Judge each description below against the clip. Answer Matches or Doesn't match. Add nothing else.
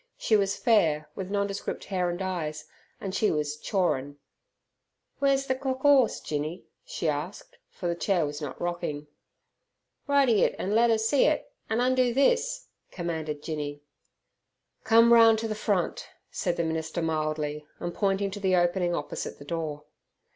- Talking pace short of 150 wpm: Doesn't match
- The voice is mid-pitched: Matches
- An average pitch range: Doesn't match